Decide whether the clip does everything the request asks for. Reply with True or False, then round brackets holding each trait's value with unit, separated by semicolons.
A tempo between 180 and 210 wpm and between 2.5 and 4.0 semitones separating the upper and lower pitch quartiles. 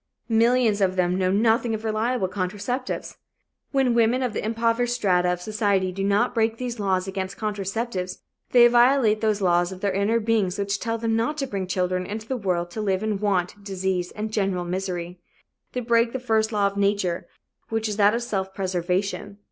True (190 wpm; 3.3 semitones)